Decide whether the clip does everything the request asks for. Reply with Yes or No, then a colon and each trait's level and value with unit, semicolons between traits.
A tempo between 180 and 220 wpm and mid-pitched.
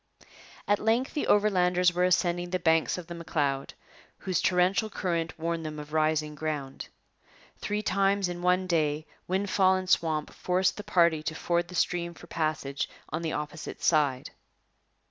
No: average, 160 wpm; medium, 170 Hz